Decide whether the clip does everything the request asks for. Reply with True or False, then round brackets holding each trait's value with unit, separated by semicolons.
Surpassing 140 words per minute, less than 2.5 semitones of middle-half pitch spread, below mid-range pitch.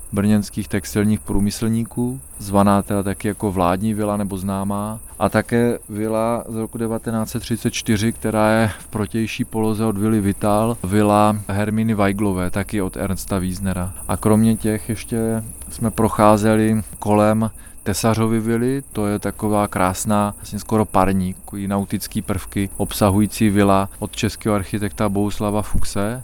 False (135 wpm; 1.8 semitones; 105 Hz)